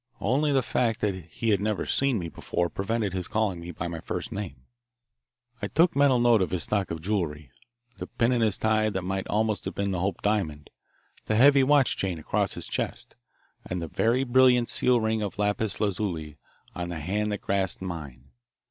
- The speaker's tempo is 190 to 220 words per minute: Yes, average, 200 wpm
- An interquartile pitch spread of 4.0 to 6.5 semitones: Yes, average, 4.5 semitones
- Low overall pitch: Yes, low, 100 Hz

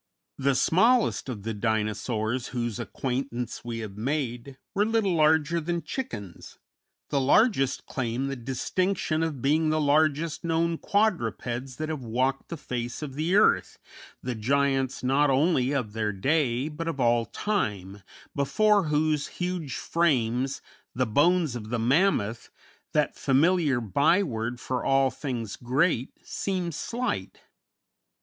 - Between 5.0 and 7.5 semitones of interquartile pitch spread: Yes, average, 5.3 semitones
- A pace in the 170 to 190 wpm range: No, slow, 135 wpm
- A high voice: No, low, 135 Hz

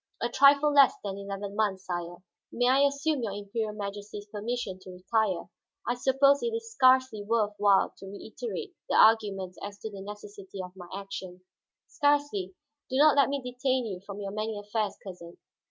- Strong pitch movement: No, average, 4.8 semitones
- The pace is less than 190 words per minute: Yes, average, 175 wpm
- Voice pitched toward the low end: No, high, 210 Hz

